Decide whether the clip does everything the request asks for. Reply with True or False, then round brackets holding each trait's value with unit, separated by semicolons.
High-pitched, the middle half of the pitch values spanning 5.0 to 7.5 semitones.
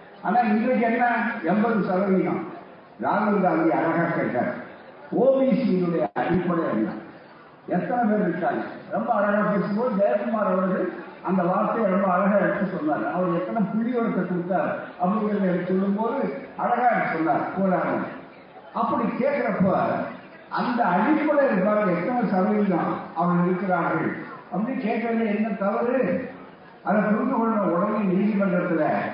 False (200 Hz; 4.2 semitones)